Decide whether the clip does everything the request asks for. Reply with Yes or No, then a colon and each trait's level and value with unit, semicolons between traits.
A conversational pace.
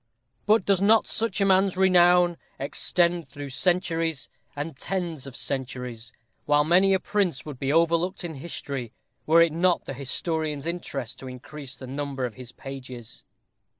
Yes: average, 155 wpm